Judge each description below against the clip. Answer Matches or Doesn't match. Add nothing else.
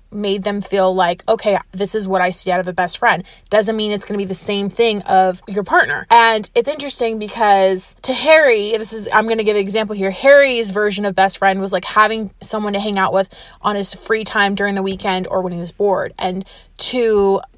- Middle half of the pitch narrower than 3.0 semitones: Matches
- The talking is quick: Matches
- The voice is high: Matches